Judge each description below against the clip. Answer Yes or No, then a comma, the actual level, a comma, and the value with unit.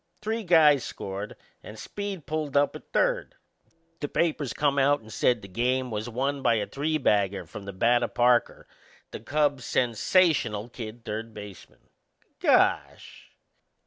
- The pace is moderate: Yes, average, 150 wpm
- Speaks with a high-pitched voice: No, low, 125 Hz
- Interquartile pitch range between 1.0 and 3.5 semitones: No, wide, 5.4 semitones